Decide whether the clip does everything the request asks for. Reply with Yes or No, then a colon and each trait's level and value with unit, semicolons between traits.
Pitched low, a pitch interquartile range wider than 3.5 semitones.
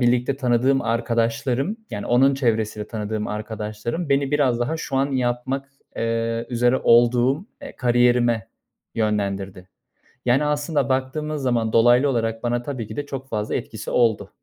No: low, 120 Hz; average, 3.0 semitones